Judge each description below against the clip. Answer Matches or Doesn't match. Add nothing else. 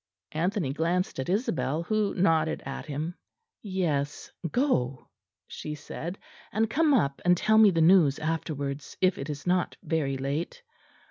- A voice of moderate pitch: Matches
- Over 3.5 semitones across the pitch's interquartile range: Matches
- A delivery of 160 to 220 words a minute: Doesn't match